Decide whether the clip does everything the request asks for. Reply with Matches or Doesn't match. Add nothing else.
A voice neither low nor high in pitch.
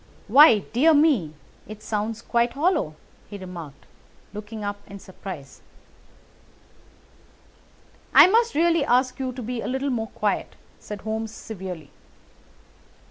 Doesn't match